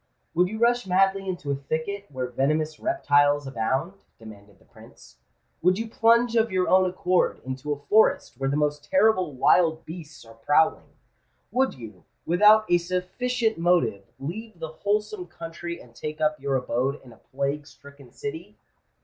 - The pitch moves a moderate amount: No, wide, 5.8 semitones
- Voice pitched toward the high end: No, medium, 160 Hz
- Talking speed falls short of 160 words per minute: No, average, 165 wpm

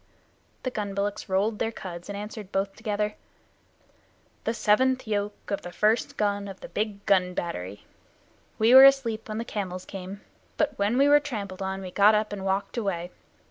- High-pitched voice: Yes, high, 205 Hz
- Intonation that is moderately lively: No, narrow, 2.3 semitones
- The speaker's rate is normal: Yes, average, 180 wpm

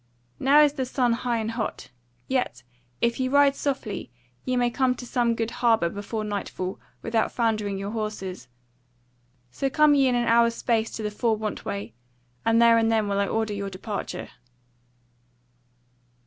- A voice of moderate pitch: No, high, 230 Hz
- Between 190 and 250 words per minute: No, average, 170 wpm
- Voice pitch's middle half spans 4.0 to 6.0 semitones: No, average, 2.9 semitones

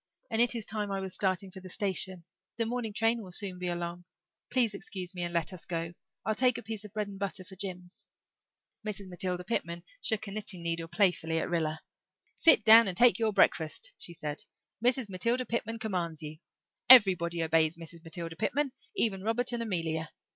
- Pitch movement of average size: Yes, average, 4.4 semitones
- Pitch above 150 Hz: Yes, high, 190 Hz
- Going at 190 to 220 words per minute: Yes, average, 195 wpm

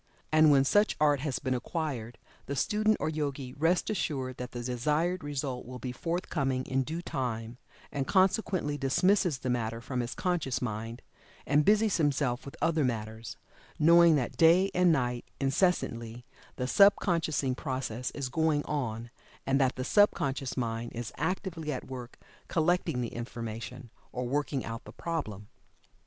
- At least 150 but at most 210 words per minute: Yes, average, 160 wpm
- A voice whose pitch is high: No, low, 135 Hz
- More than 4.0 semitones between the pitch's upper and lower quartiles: Yes, average, 4.7 semitones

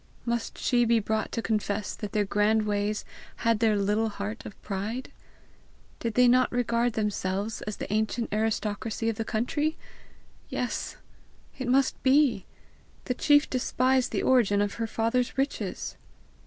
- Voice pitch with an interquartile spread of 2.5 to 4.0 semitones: Yes, average, 2.8 semitones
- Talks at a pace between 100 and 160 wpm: Yes, average, 150 wpm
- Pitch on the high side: Yes, high, 225 Hz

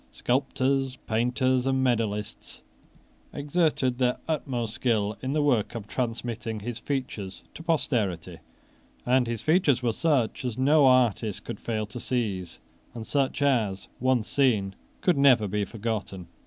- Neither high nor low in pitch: No, low, 125 Hz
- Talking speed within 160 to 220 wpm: No, average, 140 wpm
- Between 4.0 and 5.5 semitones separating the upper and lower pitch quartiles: No, average, 3.6 semitones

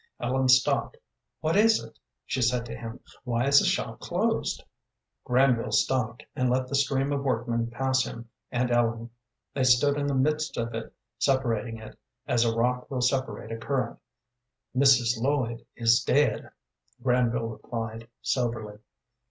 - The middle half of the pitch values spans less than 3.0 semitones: Yes, narrow, 2.4 semitones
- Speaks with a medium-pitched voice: No, low, 125 Hz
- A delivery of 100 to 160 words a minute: Yes, average, 150 wpm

